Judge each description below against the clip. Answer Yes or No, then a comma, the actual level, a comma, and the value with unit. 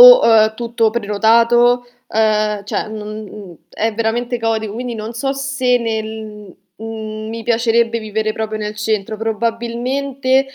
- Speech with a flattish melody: Yes, narrow, 1.7 semitones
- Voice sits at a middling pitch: No, high, 225 Hz